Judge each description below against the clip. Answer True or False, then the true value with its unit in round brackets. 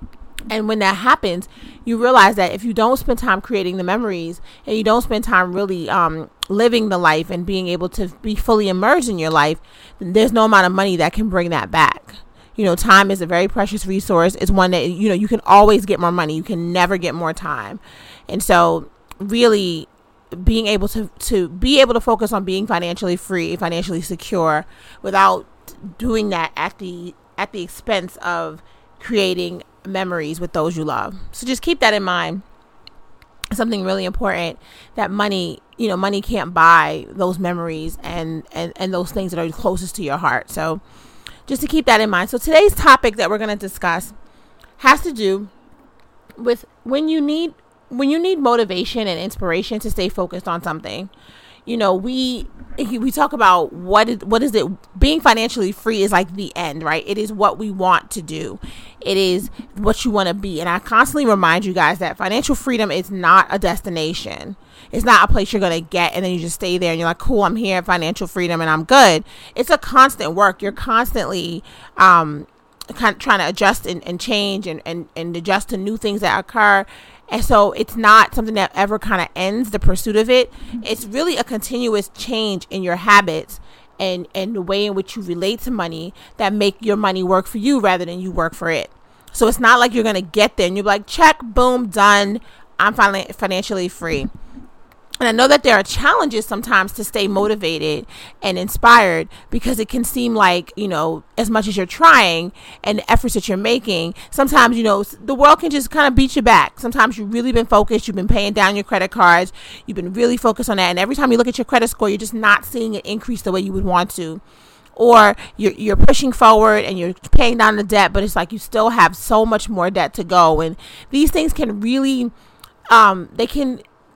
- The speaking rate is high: True (210 wpm)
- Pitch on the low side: False (200 Hz)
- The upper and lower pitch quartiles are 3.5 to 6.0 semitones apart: True (4.2 semitones)